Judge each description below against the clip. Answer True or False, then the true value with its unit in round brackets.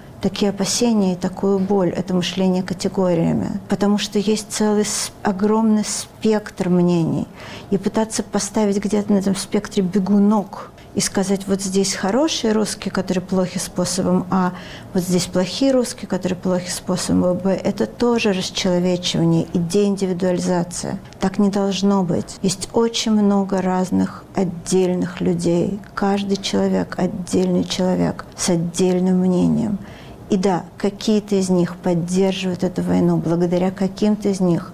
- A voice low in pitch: False (190 Hz)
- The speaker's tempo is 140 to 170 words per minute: False (130 wpm)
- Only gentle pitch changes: True (2.1 semitones)